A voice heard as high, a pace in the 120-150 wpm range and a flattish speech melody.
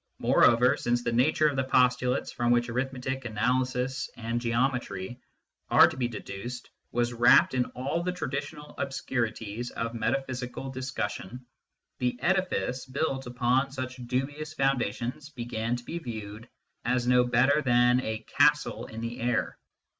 No: low, 125 Hz; average, 140 wpm; narrow, 1.9 semitones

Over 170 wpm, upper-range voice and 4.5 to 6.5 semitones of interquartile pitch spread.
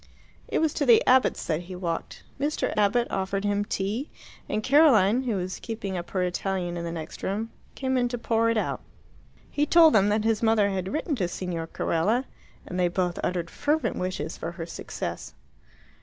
Yes: average, 190 wpm; high, 200 Hz; average, 4.9 semitones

